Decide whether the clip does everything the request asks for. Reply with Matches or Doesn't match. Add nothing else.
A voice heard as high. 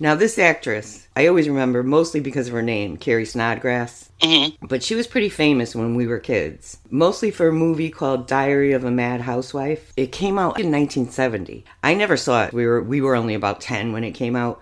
Doesn't match